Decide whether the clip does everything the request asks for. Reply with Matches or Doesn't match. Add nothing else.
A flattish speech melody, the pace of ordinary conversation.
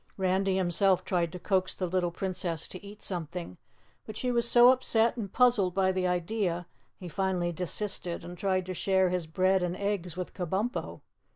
Matches